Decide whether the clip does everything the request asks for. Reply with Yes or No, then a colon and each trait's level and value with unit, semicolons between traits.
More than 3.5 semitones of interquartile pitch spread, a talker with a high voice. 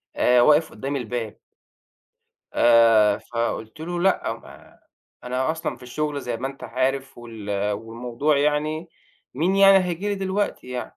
No: average, 5.2 semitones; low, 130 Hz